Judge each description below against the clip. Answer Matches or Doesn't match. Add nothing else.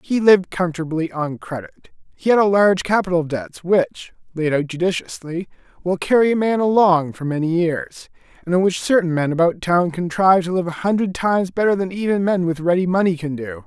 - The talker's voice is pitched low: Doesn't match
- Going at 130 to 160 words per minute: Doesn't match